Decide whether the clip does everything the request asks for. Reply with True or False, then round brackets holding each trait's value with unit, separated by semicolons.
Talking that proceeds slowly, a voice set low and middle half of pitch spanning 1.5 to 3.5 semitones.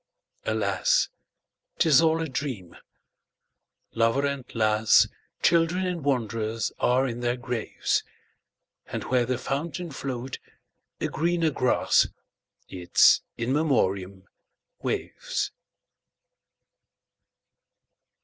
False (80 wpm; 130 Hz; 5.6 semitones)